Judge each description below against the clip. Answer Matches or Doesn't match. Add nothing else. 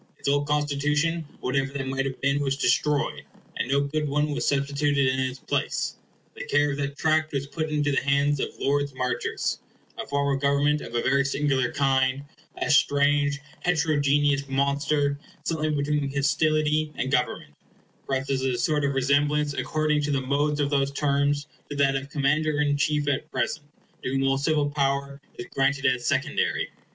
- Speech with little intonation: Matches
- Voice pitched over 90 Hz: Matches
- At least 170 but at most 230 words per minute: Matches